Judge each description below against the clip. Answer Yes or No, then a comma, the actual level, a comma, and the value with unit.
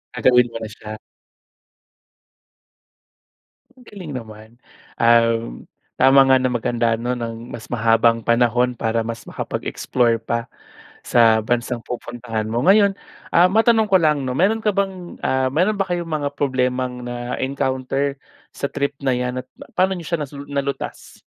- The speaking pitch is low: Yes, low, 125 Hz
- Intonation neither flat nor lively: Yes, average, 3.8 semitones